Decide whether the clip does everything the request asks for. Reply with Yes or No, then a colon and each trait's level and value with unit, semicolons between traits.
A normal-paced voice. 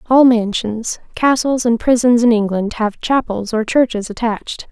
Yes: average, 155 wpm